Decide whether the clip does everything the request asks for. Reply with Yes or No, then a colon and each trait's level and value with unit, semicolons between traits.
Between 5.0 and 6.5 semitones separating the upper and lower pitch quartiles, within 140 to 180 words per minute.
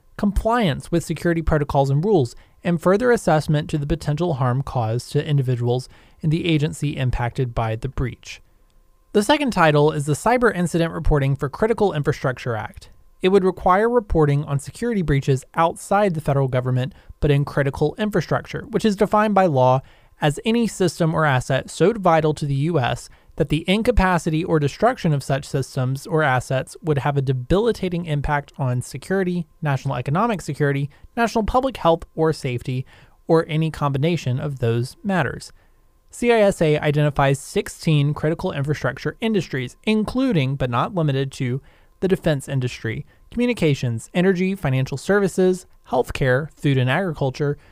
Yes: average, 5.3 semitones; average, 150 wpm